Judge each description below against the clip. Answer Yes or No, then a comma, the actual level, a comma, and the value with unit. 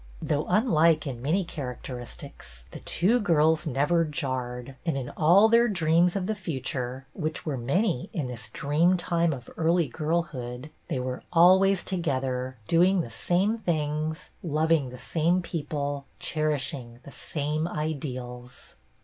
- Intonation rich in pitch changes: No, average, 4.8 semitones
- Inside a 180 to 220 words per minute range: No, average, 150 wpm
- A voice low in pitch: No, medium, 155 Hz